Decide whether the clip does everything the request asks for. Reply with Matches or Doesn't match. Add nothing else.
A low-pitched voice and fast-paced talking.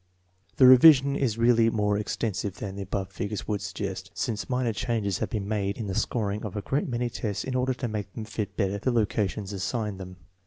Matches